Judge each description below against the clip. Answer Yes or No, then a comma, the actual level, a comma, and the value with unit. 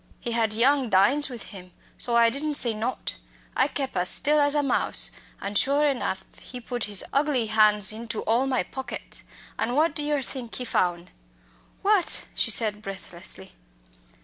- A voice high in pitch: Yes, high, 240 Hz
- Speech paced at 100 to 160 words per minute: No, average, 175 wpm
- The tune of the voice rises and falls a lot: No, average, 5.0 semitones